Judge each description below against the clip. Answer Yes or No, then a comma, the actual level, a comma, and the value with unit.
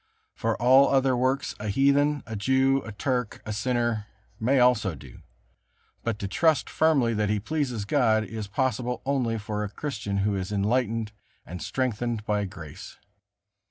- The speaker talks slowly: No, average, 160 wpm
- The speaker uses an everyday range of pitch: Yes, average, 4.0 semitones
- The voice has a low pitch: Yes, low, 115 Hz